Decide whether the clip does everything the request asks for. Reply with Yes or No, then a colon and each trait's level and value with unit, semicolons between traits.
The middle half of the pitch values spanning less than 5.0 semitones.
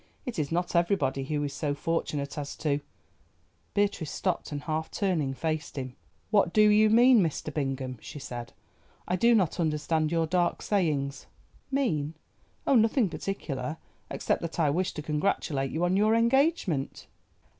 No: wide, 5.5 semitones